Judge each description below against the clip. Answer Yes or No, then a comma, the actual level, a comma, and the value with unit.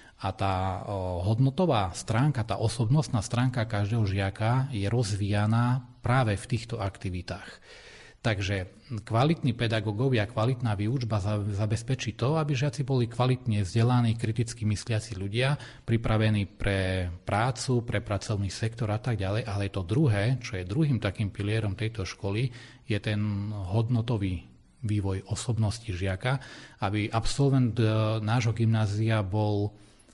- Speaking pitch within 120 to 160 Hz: No, low, 110 Hz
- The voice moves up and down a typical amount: Yes, average, 3.1 semitones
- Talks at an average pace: Yes, average, 120 wpm